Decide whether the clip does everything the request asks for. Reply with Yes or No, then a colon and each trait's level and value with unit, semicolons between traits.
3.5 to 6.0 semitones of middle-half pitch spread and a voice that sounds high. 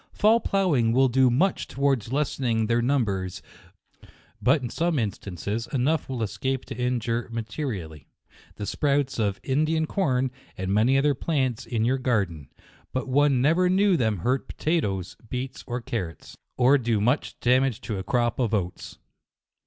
No: average, 4.1 semitones; low, 125 Hz